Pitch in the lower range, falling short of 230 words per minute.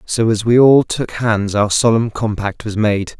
Yes: low, 110 Hz; fast, 205 wpm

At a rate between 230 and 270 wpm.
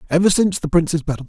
Yes: fast, 235 wpm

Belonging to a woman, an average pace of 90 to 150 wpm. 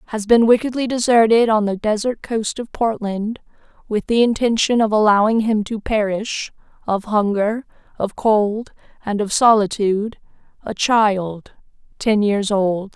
Yes: female; average, 140 wpm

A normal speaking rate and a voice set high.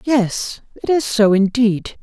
Yes: average, 150 wpm; high, 225 Hz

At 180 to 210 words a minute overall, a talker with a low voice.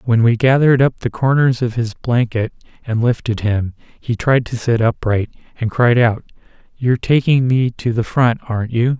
Yes: average, 185 wpm; low, 120 Hz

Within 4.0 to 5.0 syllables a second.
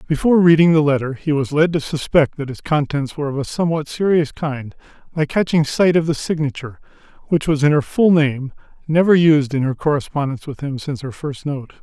No: 5.9 syllables/s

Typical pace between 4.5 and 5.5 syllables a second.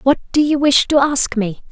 Yes: 5.0 syllables/s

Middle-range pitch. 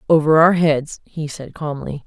Yes: medium, 150 Hz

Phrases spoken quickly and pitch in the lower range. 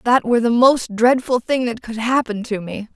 No: fast, 225 wpm; high, 235 Hz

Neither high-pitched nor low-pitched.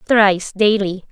No: high, 200 Hz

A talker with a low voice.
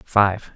Yes: low, 100 Hz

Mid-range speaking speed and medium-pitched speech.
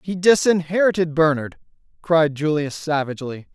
No: slow, 100 wpm; medium, 160 Hz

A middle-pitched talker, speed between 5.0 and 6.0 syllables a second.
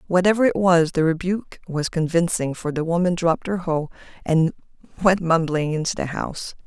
Yes: medium, 170 Hz; 5.4 syllables/s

